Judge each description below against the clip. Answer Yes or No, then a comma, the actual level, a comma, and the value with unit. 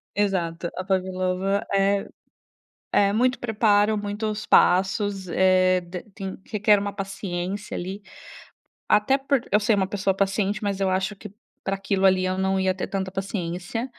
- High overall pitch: Yes, high, 195 Hz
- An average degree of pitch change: No, narrow, 1.6 semitones